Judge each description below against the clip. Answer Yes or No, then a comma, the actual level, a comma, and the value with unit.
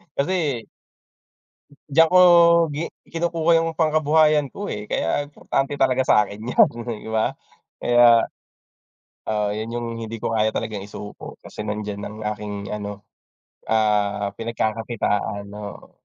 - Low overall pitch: Yes, low, 110 Hz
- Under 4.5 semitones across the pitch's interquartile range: No, wide, 5.5 semitones